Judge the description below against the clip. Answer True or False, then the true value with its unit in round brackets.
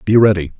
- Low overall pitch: True (100 Hz)